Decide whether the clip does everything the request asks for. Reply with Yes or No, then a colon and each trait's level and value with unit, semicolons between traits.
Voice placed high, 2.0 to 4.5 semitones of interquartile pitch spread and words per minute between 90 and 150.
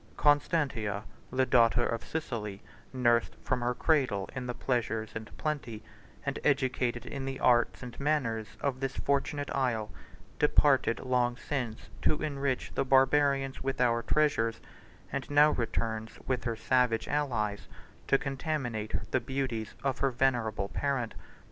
No: low, 125 Hz; average, 3.1 semitones; average, 140 wpm